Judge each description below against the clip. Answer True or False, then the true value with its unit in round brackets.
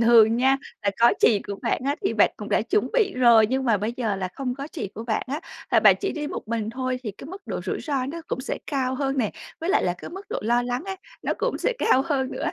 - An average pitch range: True (4.2 semitones)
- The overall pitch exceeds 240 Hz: True (255 Hz)